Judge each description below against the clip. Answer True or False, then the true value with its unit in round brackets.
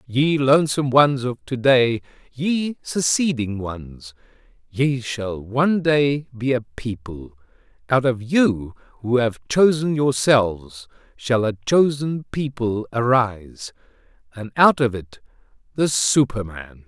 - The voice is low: True (125 Hz)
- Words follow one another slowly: True (115 wpm)